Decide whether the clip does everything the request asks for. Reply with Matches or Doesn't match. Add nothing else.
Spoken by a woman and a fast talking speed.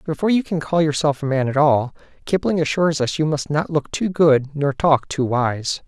Doesn't match